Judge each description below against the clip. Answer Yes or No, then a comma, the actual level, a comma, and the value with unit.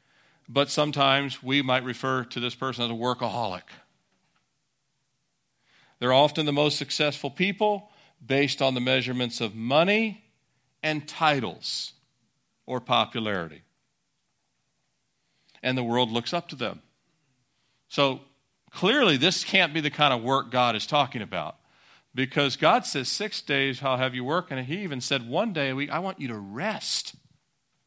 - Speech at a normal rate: Yes, average, 150 wpm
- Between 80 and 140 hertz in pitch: Yes, low, 135 Hz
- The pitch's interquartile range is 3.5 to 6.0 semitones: No, average, 3.0 semitones